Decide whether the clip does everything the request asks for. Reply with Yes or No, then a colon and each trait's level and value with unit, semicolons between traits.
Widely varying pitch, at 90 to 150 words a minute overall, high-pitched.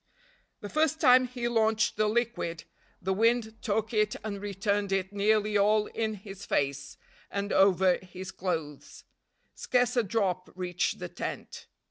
No: average, 2.8 semitones; average, 145 wpm; high, 205 Hz